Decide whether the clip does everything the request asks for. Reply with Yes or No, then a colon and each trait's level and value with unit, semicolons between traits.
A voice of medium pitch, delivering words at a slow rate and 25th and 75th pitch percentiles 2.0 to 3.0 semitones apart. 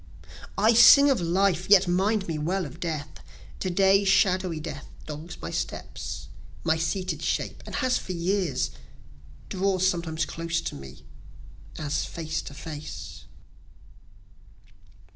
No: medium, 175 Hz; slow, 130 wpm; average, 3.5 semitones